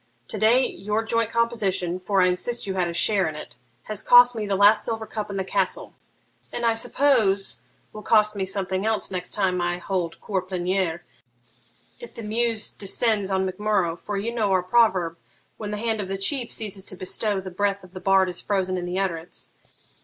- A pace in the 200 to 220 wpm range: Yes, fast, 205 wpm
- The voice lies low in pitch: No, high, 195 Hz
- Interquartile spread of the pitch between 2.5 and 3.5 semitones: Yes, average, 2.9 semitones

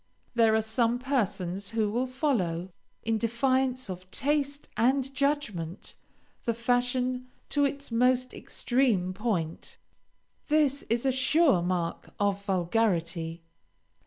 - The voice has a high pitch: Yes, high, 235 Hz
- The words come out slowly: Yes, slow, 115 wpm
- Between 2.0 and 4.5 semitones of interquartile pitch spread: No, wide, 5.6 semitones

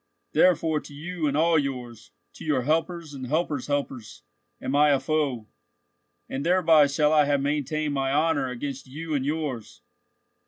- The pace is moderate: Yes, average, 160 wpm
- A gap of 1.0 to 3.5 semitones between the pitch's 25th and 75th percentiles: Yes, narrow, 2.6 semitones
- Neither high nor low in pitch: Yes, medium, 145 Hz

